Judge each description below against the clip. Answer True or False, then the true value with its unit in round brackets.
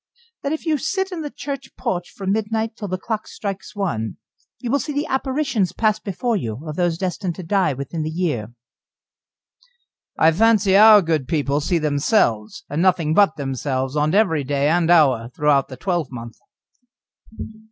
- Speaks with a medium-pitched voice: True (175 Hz)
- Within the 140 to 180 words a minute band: True (170 wpm)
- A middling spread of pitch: False (6.8 semitones)